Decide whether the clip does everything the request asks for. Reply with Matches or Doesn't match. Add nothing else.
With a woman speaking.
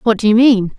Matches